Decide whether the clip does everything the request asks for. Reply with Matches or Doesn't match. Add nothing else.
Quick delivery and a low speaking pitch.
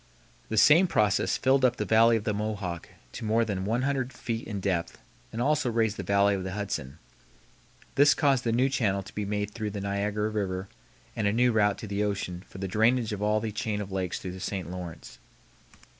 Matches